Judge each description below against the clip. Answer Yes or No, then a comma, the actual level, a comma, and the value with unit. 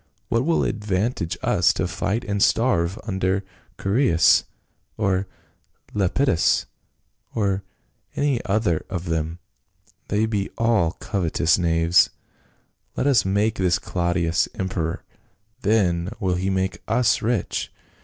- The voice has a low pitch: Yes, very low, 95 Hz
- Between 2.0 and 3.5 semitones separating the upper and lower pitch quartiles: No, average, 4.2 semitones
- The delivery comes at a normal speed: No, slow, 115 wpm